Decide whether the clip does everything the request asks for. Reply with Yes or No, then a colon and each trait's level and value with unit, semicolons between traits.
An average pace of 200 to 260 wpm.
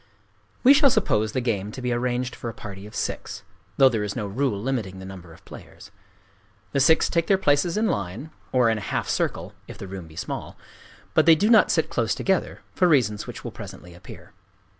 Yes: fast, 205 wpm